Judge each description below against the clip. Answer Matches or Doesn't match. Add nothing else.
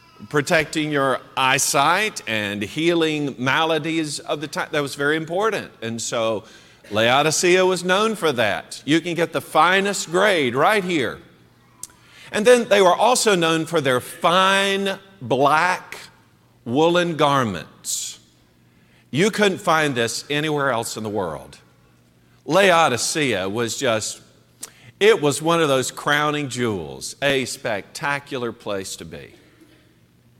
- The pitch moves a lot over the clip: Matches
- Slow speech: Matches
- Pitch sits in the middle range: Matches